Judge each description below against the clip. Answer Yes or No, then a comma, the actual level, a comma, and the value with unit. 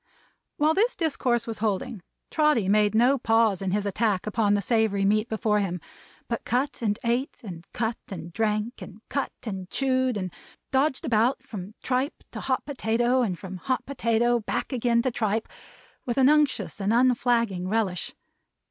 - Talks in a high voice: Yes, high, 225 Hz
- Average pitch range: Yes, average, 3.8 semitones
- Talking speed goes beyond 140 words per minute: Yes, average, 165 wpm